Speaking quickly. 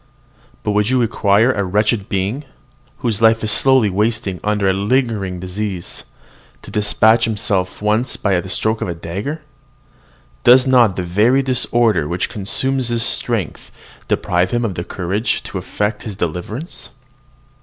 No: average, 155 wpm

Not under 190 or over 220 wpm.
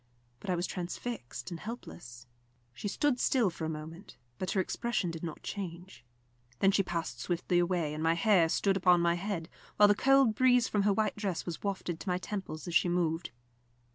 Yes: average, 200 wpm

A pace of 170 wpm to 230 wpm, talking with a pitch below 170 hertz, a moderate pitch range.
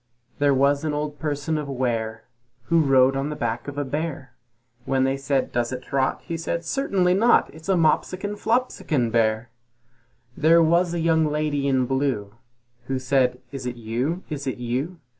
Yes: average, 180 wpm; medium, 140 Hz; average, 3.9 semitones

